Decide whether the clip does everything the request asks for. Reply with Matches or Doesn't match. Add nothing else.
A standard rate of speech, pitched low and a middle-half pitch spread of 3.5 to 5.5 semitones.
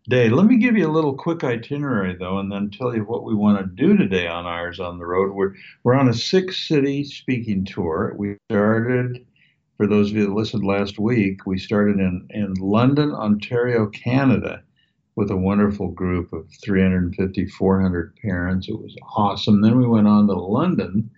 Matches